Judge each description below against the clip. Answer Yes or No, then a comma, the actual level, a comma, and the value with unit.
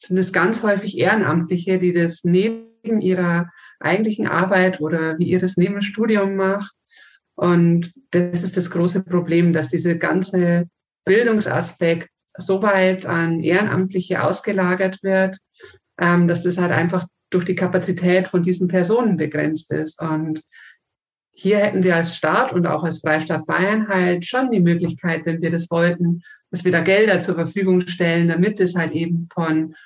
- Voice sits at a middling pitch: Yes, medium, 180 Hz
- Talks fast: No, average, 155 wpm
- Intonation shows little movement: Yes, narrow, 2.0 semitones